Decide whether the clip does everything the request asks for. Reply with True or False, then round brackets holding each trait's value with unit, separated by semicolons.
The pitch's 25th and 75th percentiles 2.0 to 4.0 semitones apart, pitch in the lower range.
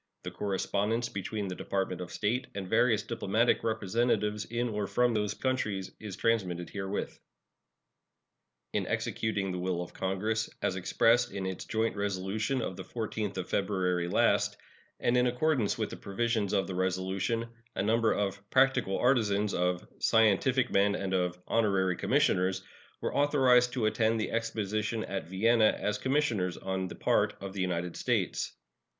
True (3.4 semitones; 105 Hz)